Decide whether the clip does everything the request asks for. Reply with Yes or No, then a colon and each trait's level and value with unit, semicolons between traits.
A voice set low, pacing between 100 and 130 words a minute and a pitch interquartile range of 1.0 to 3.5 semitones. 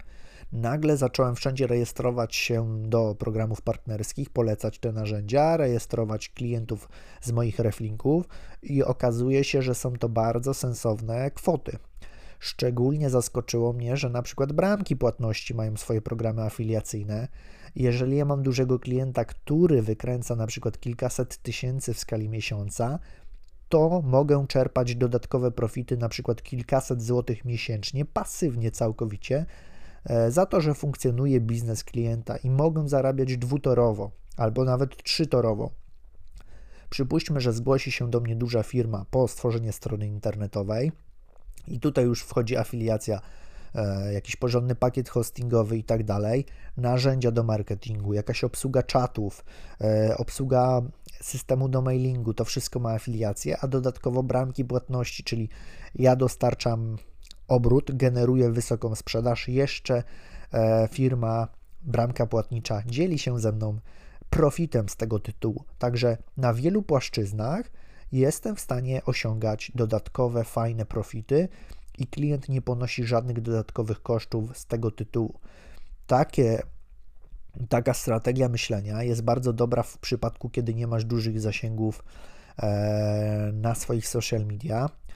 Yes: low, 120 Hz; average, 125 wpm; narrow, 2.6 semitones